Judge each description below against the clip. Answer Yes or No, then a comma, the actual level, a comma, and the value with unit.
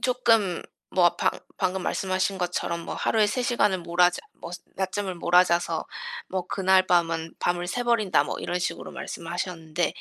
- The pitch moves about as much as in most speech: No, narrow, 1.9 semitones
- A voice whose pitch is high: No, medium, 180 Hz